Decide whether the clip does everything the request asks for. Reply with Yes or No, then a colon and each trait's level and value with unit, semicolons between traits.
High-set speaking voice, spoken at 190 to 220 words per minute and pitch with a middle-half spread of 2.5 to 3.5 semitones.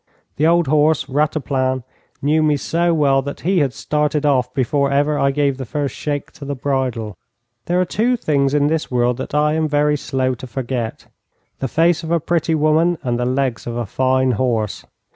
No: medium, 145 Hz; average, 200 wpm; average, 2.9 semitones